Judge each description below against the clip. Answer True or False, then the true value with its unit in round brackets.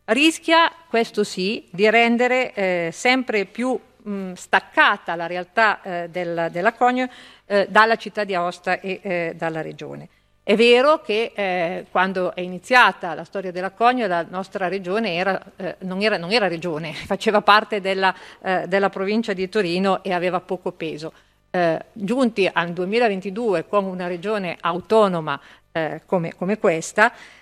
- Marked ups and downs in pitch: False (3.7 semitones)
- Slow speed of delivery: False (155 wpm)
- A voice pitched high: True (195 Hz)